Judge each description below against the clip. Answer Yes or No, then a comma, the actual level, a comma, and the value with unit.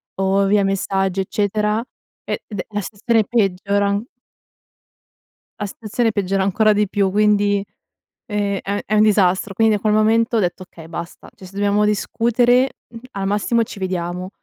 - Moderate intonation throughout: No, narrow, 1.8 semitones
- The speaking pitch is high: Yes, high, 205 Hz